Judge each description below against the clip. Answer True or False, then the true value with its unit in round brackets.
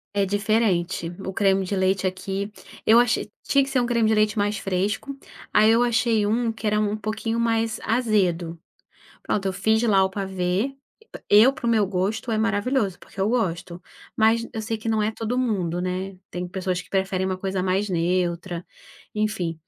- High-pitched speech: True (205 Hz)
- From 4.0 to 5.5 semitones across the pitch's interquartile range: False (3.1 semitones)